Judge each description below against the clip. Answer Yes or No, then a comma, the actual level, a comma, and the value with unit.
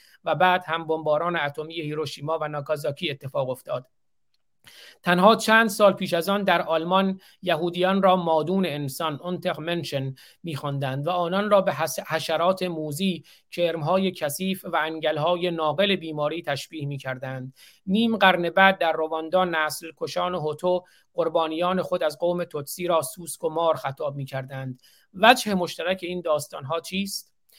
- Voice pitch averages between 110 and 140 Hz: No, medium, 165 Hz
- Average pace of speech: Yes, average, 135 wpm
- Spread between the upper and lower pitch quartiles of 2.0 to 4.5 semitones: Yes, average, 3.2 semitones